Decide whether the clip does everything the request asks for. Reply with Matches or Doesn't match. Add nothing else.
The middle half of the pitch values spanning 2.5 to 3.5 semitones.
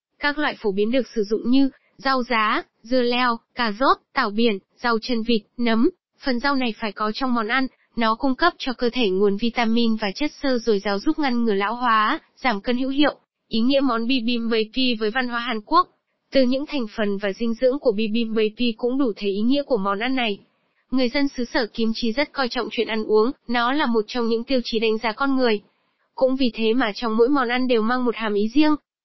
Matches